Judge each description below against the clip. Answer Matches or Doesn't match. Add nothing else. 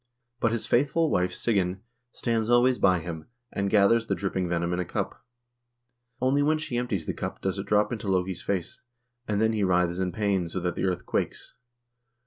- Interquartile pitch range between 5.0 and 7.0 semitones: Doesn't match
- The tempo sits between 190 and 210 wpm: Matches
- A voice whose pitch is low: Matches